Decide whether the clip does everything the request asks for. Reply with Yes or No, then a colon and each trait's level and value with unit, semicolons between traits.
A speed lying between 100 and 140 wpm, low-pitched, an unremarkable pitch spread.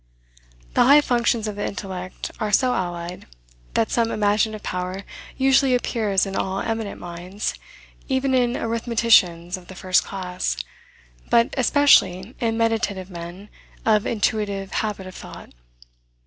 No: slow, 135 wpm; high, 210 Hz; average, 3.8 semitones